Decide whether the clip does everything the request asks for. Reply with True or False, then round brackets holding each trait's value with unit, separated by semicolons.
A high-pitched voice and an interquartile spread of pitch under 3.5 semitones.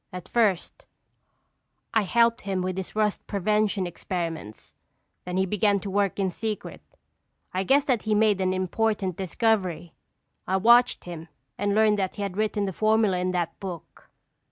True (195 Hz; 2.8 semitones)